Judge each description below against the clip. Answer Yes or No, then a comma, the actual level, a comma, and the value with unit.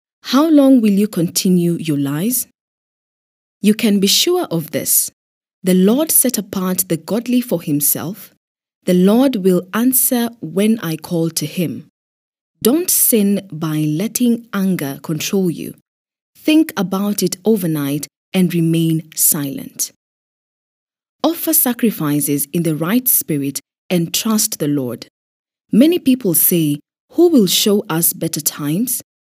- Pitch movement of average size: No, wide, 6.4 semitones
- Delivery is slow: Yes, slow, 130 wpm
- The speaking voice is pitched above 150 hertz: Yes, medium, 185 Hz